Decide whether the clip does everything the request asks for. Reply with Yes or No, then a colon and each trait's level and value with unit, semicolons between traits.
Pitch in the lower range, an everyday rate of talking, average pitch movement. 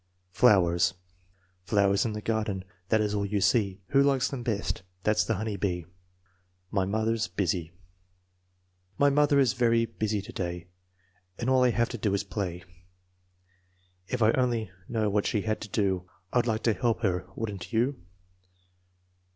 Yes: low, 105 Hz; average, 170 wpm; average, 3.5 semitones